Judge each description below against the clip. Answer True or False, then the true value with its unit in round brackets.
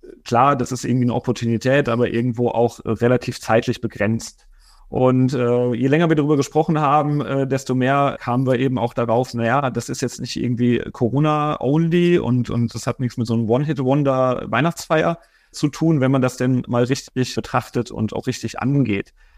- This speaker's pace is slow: False (180 wpm)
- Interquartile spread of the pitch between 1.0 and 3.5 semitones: True (2.8 semitones)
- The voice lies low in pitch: True (125 Hz)